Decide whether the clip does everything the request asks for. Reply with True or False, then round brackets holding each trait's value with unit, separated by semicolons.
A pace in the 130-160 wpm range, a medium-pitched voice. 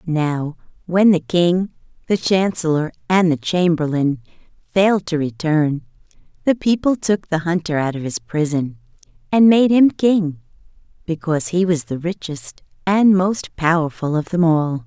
True (145 wpm; 170 Hz)